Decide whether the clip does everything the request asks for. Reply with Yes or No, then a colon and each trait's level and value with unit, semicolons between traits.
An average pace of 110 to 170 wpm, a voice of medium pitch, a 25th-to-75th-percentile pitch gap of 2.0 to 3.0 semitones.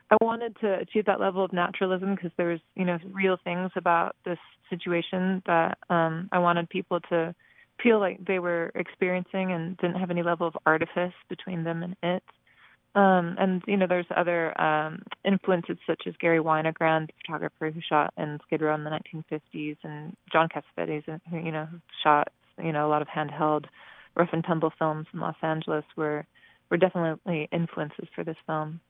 No: average, 185 wpm; medium, 170 Hz; average, 2.7 semitones